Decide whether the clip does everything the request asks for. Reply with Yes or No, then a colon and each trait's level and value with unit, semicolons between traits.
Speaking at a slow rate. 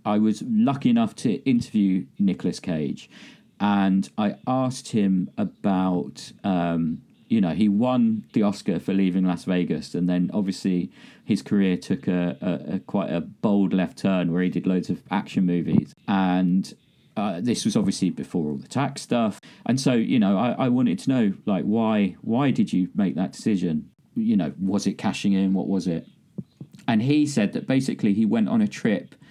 No: average, 185 wpm